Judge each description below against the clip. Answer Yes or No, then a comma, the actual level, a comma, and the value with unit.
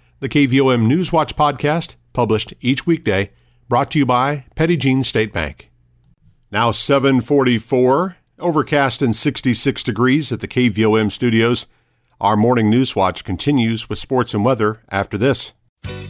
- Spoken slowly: Yes, slow, 130 wpm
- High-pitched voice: No, low, 125 Hz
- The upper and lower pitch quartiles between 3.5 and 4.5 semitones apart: Yes, average, 4.2 semitones